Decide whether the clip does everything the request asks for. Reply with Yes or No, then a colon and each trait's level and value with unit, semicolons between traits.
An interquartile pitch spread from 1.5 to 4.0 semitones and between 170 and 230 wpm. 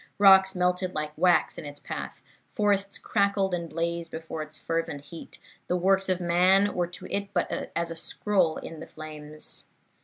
Yes: average, 3.0 semitones; average, 175 wpm